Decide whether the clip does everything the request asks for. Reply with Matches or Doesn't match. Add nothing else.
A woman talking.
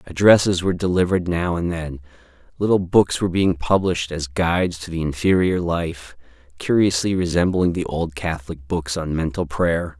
Doesn't match